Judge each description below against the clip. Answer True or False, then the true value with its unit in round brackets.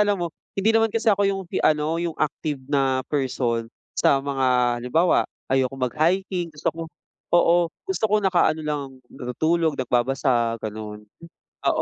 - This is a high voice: False (150 Hz)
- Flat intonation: False (5.3 semitones)